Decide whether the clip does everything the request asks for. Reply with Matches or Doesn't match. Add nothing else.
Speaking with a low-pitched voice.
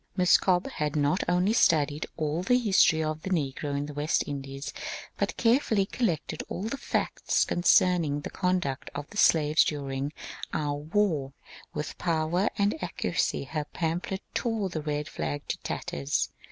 Doesn't match